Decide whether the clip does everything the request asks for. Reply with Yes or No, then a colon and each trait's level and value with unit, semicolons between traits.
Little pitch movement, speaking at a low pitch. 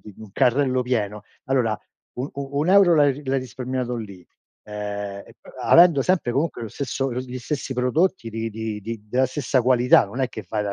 No: average, 3.5 semitones; low, 125 Hz